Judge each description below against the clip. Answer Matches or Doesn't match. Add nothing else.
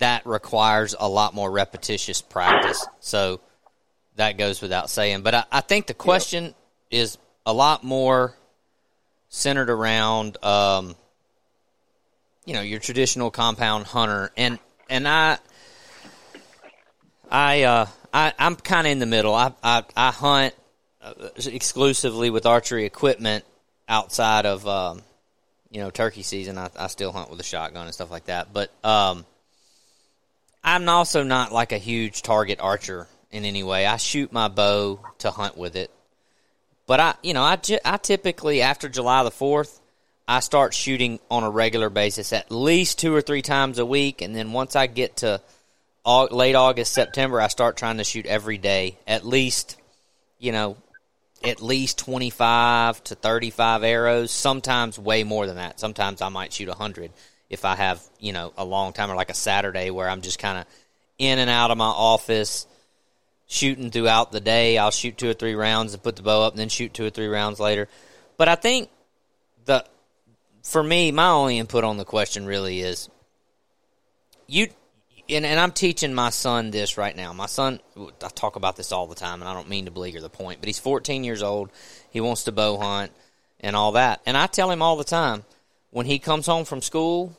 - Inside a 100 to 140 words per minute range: Doesn't match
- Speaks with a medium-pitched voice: Doesn't match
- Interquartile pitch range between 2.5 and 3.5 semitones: Doesn't match